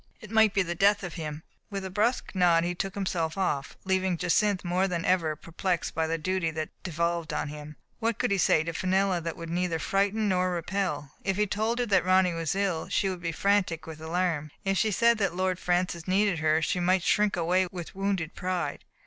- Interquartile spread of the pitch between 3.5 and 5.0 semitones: No, average, 2.8 semitones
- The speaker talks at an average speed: No, fast, 220 wpm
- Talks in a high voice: No, medium, 180 Hz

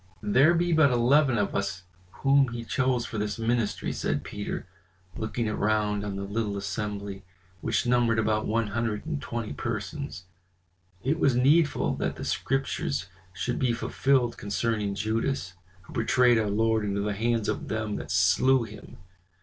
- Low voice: Yes, low, 110 Hz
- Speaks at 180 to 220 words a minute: No, average, 160 wpm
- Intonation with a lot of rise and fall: No, average, 3.2 semitones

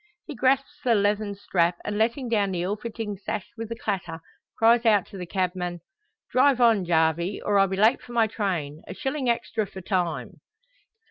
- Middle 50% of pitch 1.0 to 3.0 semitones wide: No, average, 4.1 semitones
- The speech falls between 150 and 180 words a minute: No, average, 190 wpm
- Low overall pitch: No, high, 205 Hz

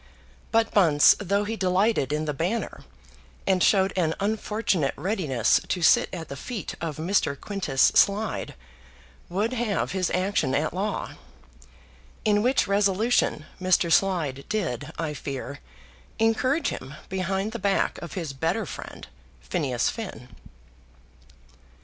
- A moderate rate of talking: No, slow, 130 wpm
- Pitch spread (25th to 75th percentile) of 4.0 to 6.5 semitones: Yes, average, 5.3 semitones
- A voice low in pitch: No, medium, 185 Hz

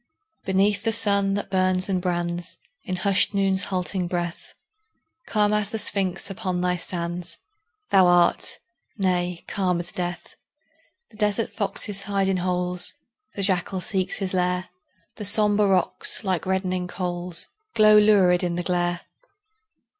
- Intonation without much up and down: Yes, narrow, 2.1 semitones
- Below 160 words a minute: Yes, average, 140 wpm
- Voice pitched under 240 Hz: Yes, medium, 185 Hz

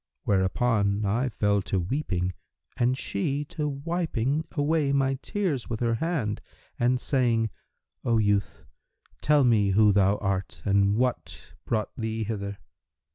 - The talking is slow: Yes, slow, 130 wpm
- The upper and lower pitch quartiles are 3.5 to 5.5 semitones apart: Yes, average, 5.2 semitones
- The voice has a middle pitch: No, low, 115 Hz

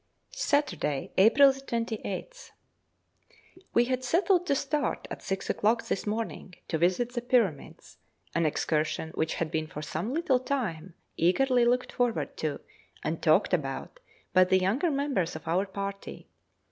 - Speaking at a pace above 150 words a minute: No, average, 145 wpm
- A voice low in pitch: No, high, 220 Hz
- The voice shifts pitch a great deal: Yes, wide, 6.9 semitones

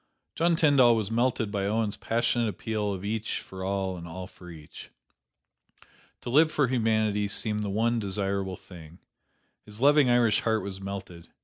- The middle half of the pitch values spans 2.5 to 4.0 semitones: Yes, average, 3.3 semitones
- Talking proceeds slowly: No, average, 165 wpm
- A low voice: Yes, low, 105 Hz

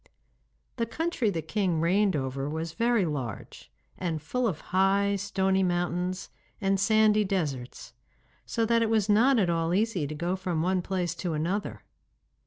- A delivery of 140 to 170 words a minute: Yes, average, 160 wpm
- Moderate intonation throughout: Yes, average, 4.2 semitones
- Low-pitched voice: No, medium, 185 Hz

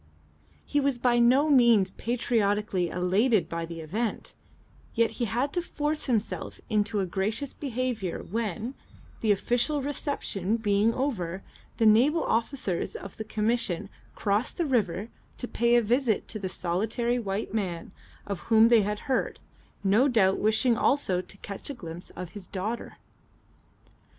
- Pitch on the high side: Yes, high, 220 Hz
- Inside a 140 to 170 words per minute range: Yes, average, 150 wpm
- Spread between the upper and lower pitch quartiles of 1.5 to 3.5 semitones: No, average, 3.9 semitones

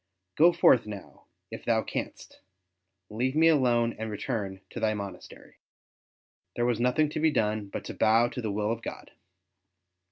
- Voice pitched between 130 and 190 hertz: No, low, 115 Hz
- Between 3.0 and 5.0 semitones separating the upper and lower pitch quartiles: Yes, average, 3.5 semitones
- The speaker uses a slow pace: No, average, 165 wpm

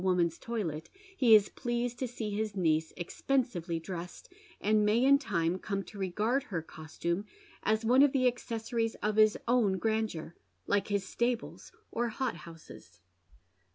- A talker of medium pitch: No, high, 210 Hz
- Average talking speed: Yes, average, 155 wpm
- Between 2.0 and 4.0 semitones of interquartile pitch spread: No, wide, 5.4 semitones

